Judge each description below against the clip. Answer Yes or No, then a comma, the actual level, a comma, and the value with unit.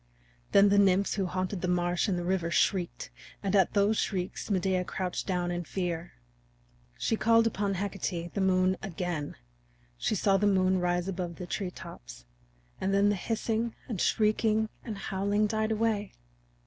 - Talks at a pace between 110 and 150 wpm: No, average, 160 wpm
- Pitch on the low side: No, high, 190 Hz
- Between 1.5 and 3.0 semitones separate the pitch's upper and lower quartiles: Yes, narrow, 2.5 semitones